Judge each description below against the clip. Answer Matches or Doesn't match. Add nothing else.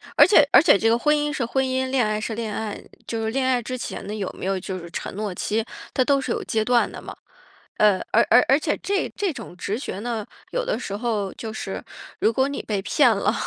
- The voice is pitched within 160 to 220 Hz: Doesn't match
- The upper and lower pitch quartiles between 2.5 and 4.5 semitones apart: Matches